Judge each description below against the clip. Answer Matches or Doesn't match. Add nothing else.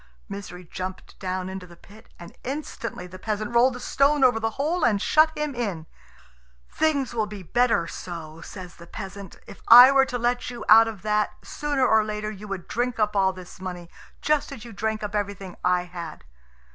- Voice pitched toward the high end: Matches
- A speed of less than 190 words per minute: Doesn't match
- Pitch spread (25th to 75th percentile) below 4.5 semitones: Doesn't match